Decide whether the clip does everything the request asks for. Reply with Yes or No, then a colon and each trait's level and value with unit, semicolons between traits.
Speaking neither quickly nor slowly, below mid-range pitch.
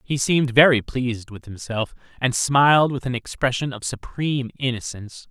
Yes: average, 160 wpm; low, 125 Hz